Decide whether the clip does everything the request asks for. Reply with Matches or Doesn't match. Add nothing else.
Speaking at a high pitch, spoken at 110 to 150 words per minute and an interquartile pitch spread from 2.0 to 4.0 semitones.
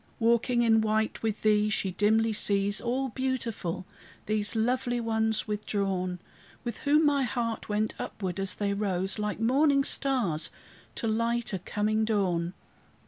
Matches